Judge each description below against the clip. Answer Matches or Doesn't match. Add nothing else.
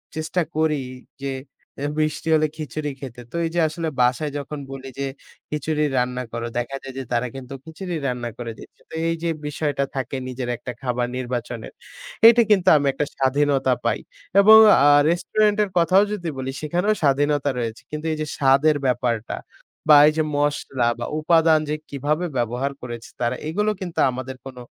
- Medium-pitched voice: Matches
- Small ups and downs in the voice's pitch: Doesn't match